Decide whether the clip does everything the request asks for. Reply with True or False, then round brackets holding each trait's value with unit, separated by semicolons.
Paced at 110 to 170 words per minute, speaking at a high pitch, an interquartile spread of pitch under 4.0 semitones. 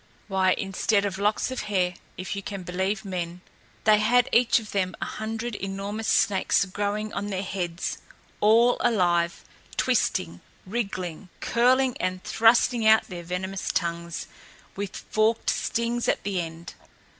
True (145 wpm; 200 Hz; 3.1 semitones)